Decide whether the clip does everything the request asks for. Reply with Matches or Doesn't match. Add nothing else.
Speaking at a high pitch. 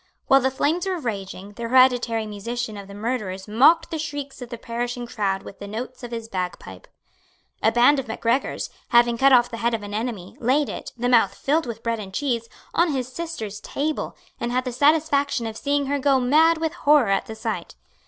Matches